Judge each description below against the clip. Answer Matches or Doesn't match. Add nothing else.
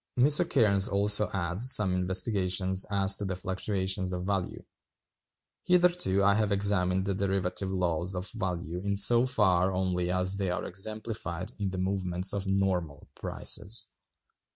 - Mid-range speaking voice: Doesn't match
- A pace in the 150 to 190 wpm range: Doesn't match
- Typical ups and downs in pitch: Doesn't match